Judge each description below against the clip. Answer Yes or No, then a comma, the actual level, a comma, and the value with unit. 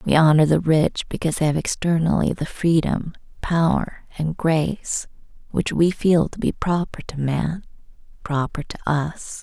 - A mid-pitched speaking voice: Yes, medium, 160 Hz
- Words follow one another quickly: No, average, 155 wpm